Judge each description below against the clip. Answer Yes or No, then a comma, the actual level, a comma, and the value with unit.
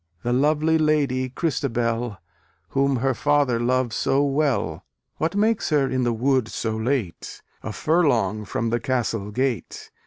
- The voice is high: No, low, 130 Hz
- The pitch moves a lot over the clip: No, average, 3.8 semitones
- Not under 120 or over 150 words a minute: Yes, average, 145 wpm